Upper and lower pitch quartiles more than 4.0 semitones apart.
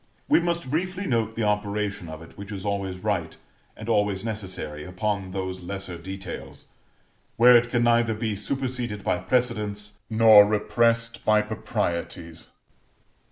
No: average, 3.4 semitones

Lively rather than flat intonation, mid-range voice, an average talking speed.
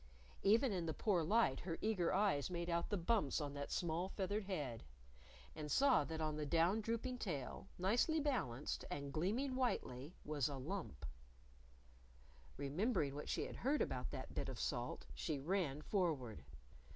Yes: wide, 6.4 semitones; medium, 170 Hz; average, 165 wpm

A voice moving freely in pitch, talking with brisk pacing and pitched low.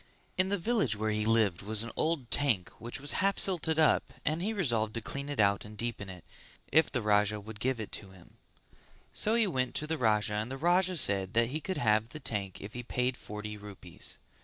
Yes: wide, 6.5 semitones; fast, 225 wpm; low, 115 Hz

